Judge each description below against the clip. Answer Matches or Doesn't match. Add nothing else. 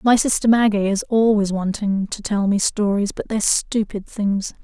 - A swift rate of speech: Doesn't match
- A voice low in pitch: Doesn't match